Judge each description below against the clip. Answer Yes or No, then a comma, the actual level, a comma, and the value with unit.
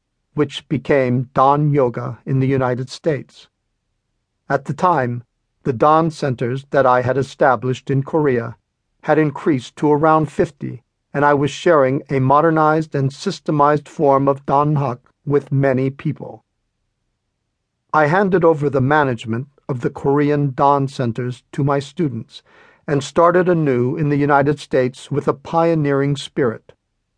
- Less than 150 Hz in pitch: Yes, medium, 140 Hz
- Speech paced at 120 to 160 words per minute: Yes, average, 140 wpm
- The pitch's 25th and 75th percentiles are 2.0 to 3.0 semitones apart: Yes, narrow, 2.5 semitones